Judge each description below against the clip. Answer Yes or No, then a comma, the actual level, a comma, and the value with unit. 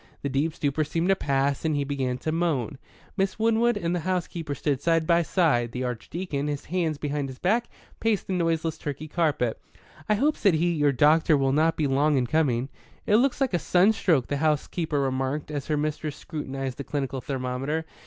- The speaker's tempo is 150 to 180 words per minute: No, average, 195 wpm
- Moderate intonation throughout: Yes, average, 3.7 semitones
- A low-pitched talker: No, medium, 150 Hz